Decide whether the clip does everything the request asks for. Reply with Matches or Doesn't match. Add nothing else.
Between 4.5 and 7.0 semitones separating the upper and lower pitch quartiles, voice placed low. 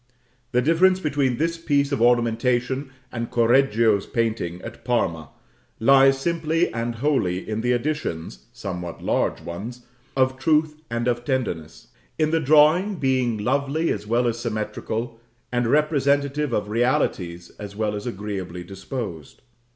Matches